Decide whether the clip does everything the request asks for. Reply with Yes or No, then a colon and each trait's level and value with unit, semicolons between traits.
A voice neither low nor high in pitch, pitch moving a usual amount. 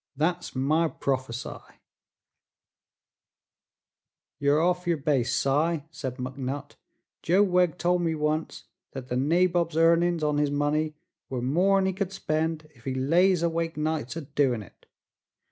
Yes: medium, 155 Hz; average, 3.8 semitones